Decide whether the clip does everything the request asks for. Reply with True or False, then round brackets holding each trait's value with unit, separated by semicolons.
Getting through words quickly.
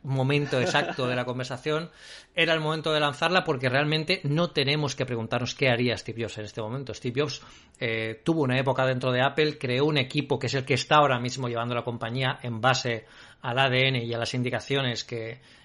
True (205 wpm)